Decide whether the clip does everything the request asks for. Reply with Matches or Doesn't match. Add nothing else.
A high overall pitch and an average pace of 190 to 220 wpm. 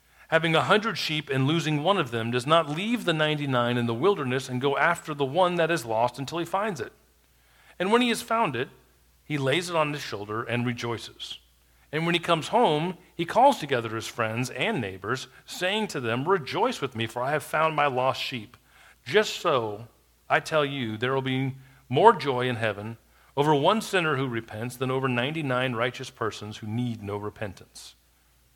Doesn't match